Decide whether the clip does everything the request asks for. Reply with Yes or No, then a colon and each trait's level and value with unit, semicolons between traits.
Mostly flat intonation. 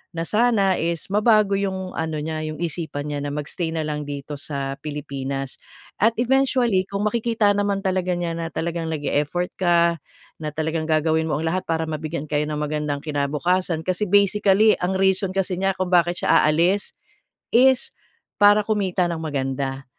No: average, 4.4 semitones